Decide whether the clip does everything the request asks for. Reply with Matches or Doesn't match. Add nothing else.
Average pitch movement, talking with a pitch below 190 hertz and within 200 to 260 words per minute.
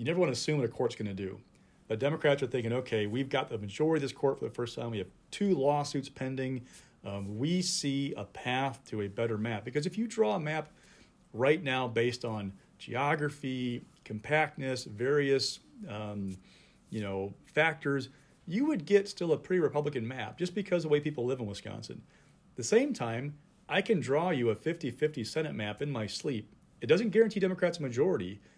Matches